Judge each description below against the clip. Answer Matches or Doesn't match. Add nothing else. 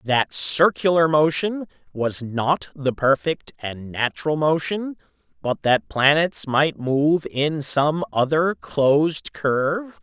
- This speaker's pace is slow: Matches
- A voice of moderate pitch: Matches